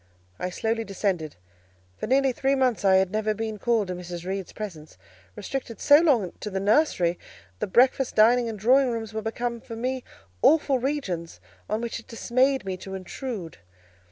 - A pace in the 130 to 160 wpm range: No, average, 175 wpm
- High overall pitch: Yes, high, 225 Hz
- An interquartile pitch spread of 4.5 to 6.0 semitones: Yes, average, 4.8 semitones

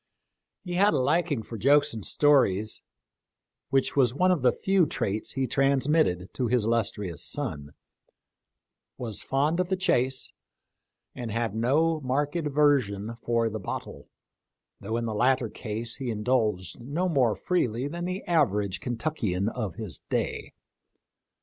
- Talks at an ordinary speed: Yes, average, 145 wpm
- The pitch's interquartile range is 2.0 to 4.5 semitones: No, average, 5.2 semitones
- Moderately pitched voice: No, low, 125 Hz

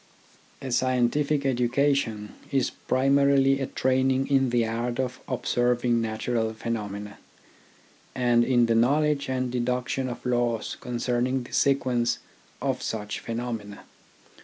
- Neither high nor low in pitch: No, low, 125 Hz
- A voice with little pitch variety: Yes, narrow, 2.0 semitones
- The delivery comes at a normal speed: No, slow, 120 wpm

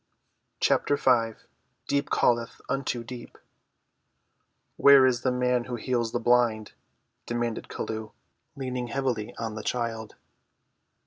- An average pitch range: No, narrow, 2.0 semitones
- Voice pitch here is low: Yes, low, 120 Hz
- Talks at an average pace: No, slow, 115 wpm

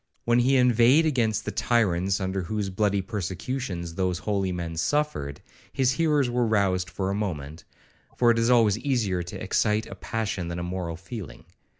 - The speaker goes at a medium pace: Yes, average, 175 wpm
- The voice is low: Yes, low, 105 Hz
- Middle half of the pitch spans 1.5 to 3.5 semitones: No, average, 4.8 semitones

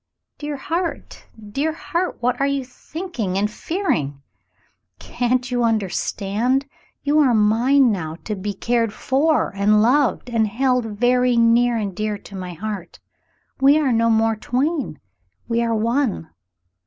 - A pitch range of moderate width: Yes, average, 4.4 semitones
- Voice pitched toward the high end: Yes, high, 235 Hz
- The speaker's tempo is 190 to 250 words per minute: No, average, 140 wpm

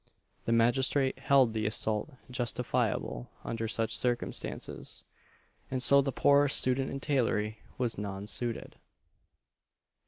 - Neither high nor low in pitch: No, low, 120 Hz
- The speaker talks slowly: Yes, slow, 115 wpm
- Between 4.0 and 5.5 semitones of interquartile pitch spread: No, average, 3.2 semitones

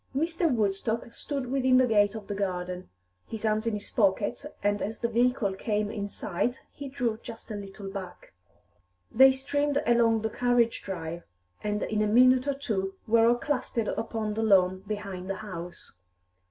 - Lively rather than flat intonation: No, average, 3.6 semitones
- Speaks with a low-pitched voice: No, high, 220 Hz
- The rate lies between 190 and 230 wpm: No, average, 175 wpm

